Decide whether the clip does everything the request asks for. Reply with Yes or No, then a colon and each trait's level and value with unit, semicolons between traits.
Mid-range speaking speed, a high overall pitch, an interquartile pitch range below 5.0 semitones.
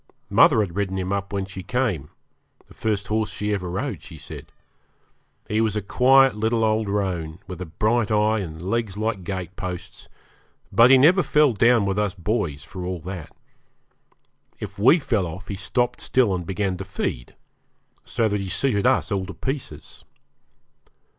No: average, 175 wpm; low, 100 Hz; average, 3.6 semitones